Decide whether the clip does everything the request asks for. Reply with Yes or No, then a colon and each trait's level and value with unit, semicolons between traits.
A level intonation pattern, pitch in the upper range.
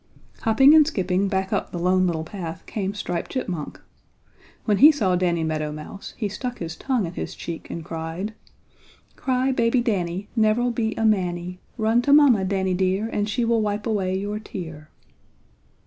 No: average, 4.3 semitones; high, 195 Hz